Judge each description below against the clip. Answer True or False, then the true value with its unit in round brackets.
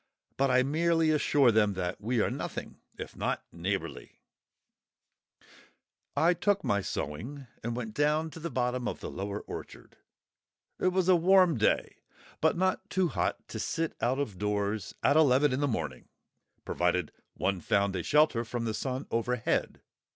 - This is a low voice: True (125 Hz)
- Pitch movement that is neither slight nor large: False (7.2 semitones)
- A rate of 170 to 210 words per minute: False (160 wpm)